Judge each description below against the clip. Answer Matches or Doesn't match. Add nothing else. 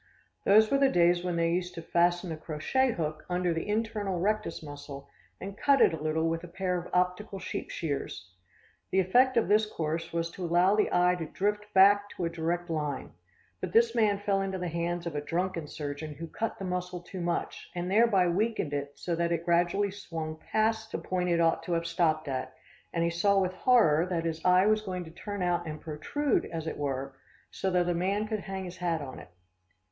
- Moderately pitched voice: Matches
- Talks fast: Matches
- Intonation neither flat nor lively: Matches